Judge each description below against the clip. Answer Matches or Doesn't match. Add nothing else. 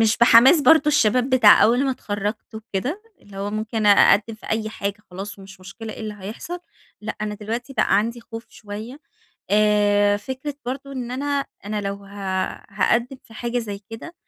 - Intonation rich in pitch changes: Doesn't match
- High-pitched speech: Matches